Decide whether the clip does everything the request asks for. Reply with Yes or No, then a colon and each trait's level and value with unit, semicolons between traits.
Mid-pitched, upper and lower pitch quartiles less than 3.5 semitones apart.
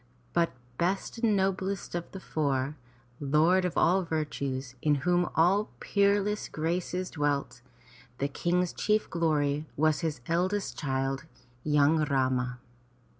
No: medium, 160 Hz; average, 4.4 semitones